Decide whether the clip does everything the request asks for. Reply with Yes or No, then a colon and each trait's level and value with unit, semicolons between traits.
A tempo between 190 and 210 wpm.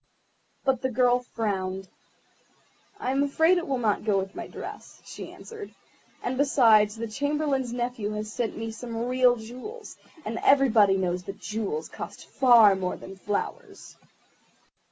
No: average, 150 wpm